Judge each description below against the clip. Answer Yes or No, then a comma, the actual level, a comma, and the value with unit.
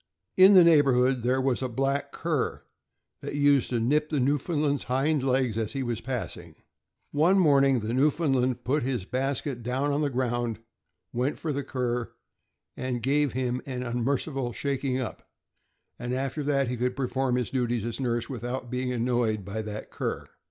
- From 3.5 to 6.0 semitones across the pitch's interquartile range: No, narrow, 2.5 semitones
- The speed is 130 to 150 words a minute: No, average, 170 wpm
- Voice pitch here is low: Yes, low, 130 Hz